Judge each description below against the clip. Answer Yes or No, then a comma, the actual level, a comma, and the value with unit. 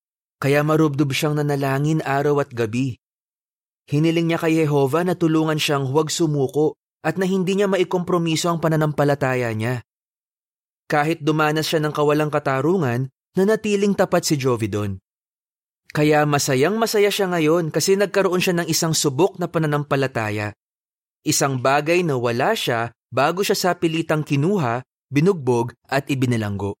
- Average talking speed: Yes, average, 135 wpm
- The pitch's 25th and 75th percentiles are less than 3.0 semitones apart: No, average, 4.0 semitones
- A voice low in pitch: No, medium, 155 Hz